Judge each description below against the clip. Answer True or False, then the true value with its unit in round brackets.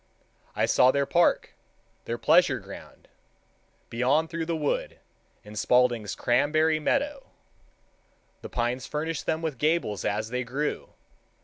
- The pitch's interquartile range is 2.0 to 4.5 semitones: False (4.9 semitones)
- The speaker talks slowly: True (125 wpm)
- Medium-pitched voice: True (145 Hz)